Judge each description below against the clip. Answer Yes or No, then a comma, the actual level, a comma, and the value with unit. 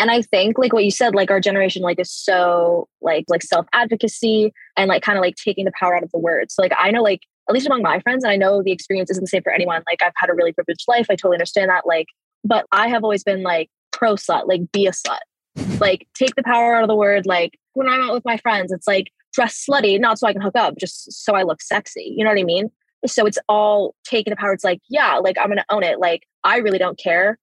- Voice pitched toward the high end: Yes, high, 200 Hz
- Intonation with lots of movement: No, average, 4.0 semitones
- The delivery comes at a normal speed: No, fast, 280 wpm